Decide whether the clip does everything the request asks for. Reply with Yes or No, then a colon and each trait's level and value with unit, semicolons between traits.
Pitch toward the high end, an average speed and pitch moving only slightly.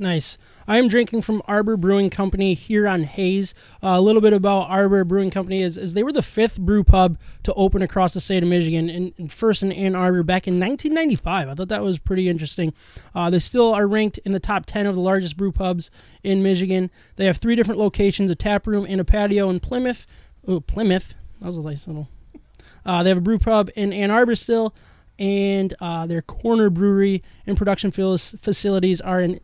No: high, 195 Hz; fast, 215 wpm; narrow, 2.2 semitones